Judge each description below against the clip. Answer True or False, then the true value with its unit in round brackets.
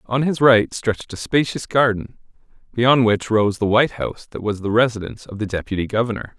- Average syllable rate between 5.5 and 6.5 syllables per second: True (5.8 syllables/s)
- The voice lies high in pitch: False (115 Hz)